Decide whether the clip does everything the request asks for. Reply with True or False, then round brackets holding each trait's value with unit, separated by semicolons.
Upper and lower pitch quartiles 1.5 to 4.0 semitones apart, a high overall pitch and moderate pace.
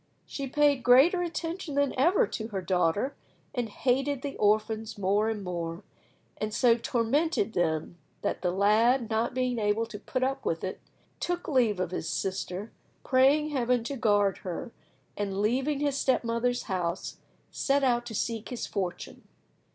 False (4.9 semitones; 230 Hz; 160 wpm)